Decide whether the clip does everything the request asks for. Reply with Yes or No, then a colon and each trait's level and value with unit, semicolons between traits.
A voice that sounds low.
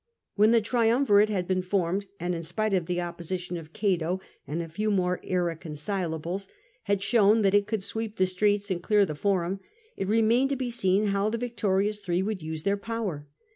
No: high, 195 Hz